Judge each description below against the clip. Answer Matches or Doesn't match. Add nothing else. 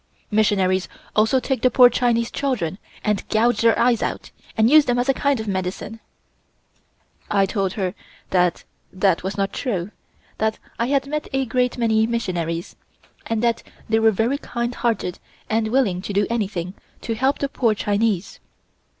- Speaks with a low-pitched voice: Doesn't match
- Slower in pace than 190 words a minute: Matches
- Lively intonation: Doesn't match